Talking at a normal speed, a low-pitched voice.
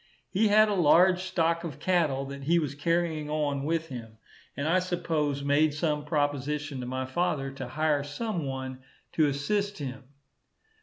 No: average, 165 wpm; medium, 150 Hz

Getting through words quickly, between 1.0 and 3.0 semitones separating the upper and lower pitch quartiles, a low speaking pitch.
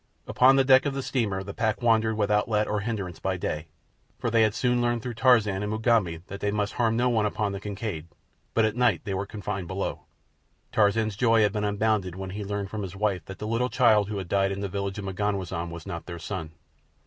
Yes: fast, 235 wpm; narrow, 2.6 semitones; low, 105 Hz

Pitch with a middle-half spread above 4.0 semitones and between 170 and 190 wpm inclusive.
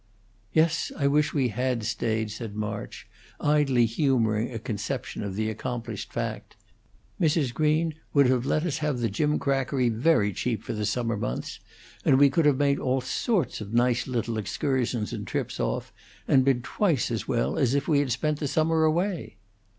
Yes: average, 4.5 semitones; average, 175 wpm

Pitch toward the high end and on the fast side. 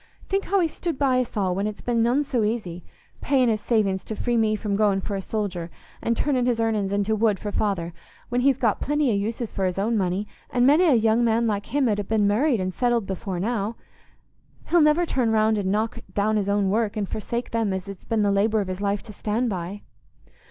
Yes: high, 215 Hz; fast, 230 wpm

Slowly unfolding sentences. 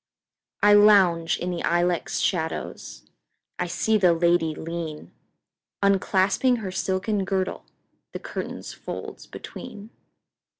Yes: slow, 90 wpm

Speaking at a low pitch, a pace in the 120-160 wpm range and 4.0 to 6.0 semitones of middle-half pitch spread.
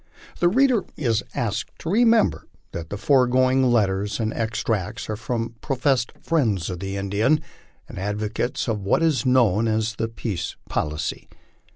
Yes: low, 115 Hz; average, 150 wpm; average, 4.3 semitones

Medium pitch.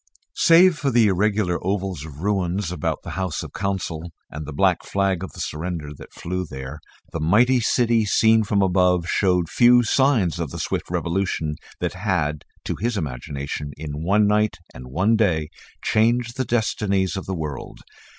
No: very low, 95 Hz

